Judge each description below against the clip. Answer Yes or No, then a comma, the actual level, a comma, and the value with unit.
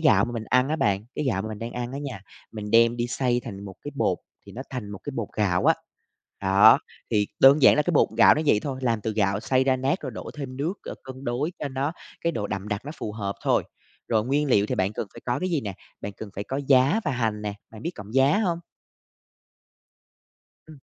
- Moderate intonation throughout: Yes, average, 4.7 semitones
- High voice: No, low, 120 Hz